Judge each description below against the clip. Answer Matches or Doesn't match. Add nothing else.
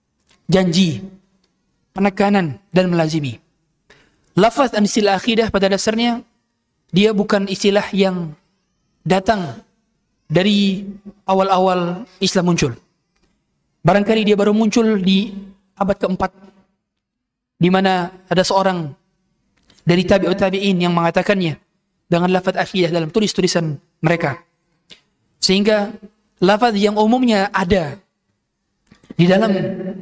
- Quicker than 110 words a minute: Doesn't match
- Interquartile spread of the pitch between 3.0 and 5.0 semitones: Doesn't match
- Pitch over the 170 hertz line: Matches